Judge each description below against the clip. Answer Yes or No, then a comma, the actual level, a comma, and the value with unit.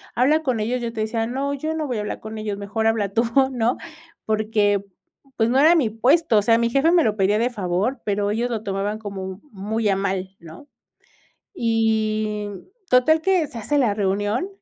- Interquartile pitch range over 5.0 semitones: No, average, 3.5 semitones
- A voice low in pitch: No, high, 220 Hz